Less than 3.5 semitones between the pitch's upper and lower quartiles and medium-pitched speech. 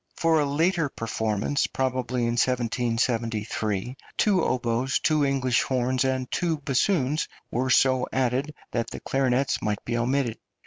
No: average, 2.7 semitones; low, 130 Hz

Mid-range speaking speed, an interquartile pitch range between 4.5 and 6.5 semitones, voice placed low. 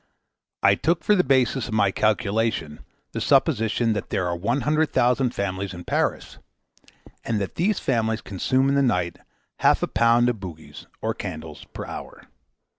Yes: average, 170 wpm; average, 5.0 semitones; low, 115 Hz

